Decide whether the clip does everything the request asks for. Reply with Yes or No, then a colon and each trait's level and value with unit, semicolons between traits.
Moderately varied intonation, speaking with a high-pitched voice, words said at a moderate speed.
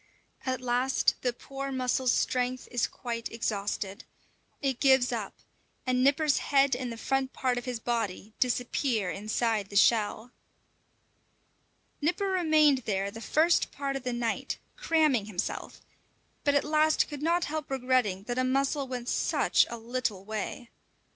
Yes: average, 3.1 semitones; very high, 250 Hz; average, 145 wpm